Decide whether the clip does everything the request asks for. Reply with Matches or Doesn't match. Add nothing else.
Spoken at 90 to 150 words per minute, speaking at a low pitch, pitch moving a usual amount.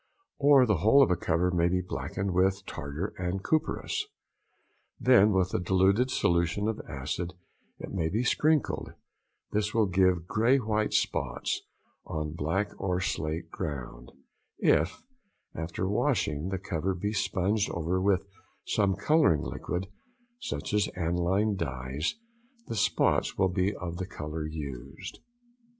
Matches